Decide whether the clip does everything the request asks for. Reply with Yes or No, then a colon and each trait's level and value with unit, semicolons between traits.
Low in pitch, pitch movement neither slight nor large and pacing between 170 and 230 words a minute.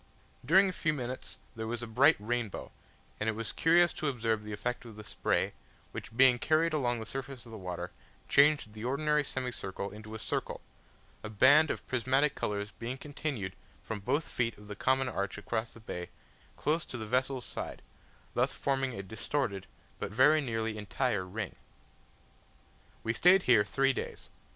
Yes: low, 120 Hz; average, 4.3 semitones; average, 175 wpm